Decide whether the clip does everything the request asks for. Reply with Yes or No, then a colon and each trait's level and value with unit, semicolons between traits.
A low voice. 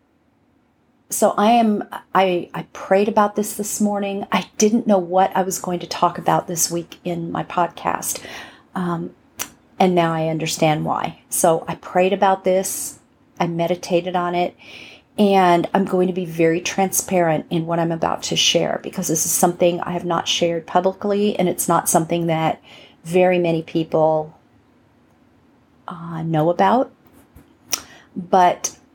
No: medium, 180 Hz